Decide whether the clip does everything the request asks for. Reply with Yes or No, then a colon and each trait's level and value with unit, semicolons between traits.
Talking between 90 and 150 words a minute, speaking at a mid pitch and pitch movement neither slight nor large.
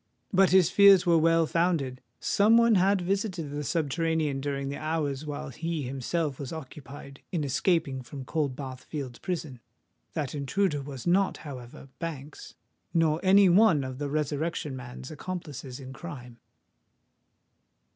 Yes: slow, 135 wpm; medium, 150 Hz; average, 4.1 semitones